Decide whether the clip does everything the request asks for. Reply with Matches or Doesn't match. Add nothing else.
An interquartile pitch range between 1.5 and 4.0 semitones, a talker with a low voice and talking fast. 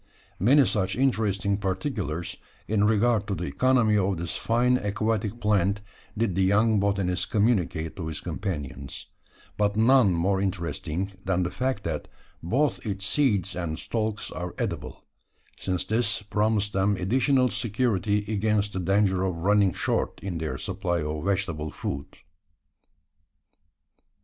Doesn't match